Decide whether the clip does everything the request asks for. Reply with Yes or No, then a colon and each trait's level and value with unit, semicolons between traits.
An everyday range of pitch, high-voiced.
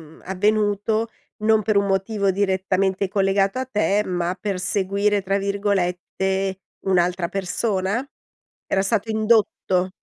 No: narrow, 1.8 semitones; high, 195 Hz